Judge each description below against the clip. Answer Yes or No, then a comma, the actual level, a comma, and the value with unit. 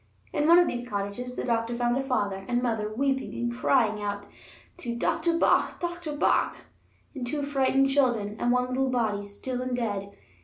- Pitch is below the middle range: No, high, 245 Hz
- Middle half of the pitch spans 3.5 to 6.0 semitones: Yes, average, 3.9 semitones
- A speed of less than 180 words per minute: No, average, 185 wpm